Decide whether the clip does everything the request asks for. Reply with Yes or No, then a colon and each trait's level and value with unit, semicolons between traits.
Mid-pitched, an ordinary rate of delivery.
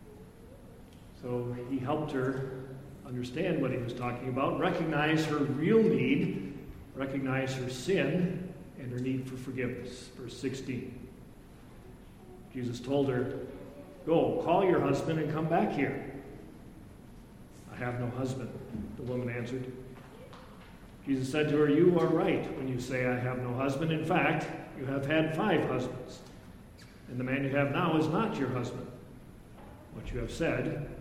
No: low, 130 Hz; average, 150 wpm